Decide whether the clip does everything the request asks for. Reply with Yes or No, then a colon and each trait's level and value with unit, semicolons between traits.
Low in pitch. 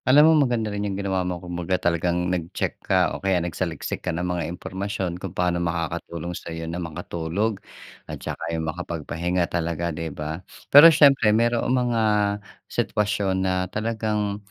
Yes: very low, 90 Hz